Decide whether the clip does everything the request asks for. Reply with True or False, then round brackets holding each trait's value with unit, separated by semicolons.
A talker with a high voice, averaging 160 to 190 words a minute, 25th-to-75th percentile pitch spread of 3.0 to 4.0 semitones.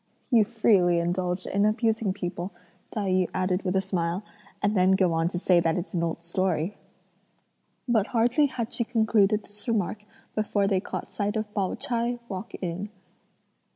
True (195 Hz; 170 wpm; 3.3 semitones)